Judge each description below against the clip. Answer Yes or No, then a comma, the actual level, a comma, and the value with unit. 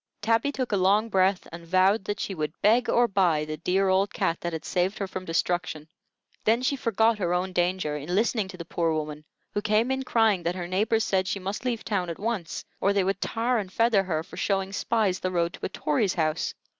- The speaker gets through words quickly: Yes, fast, 230 wpm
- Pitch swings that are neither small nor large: Yes, average, 3.7 semitones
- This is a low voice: No, high, 190 Hz